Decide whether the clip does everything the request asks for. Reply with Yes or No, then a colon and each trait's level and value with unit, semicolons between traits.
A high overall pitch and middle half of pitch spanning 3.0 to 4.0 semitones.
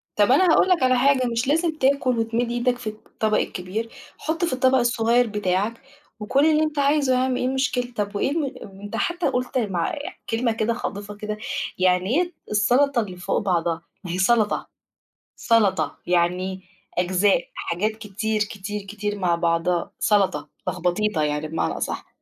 No: high, 215 Hz; average, 5.1 semitones